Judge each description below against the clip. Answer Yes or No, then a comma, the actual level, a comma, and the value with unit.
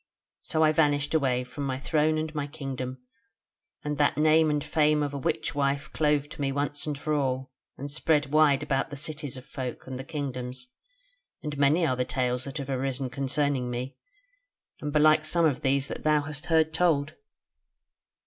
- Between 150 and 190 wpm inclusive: Yes, average, 185 wpm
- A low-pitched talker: No, medium, 145 Hz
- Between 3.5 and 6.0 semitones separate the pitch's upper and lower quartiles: No, narrow, 2.4 semitones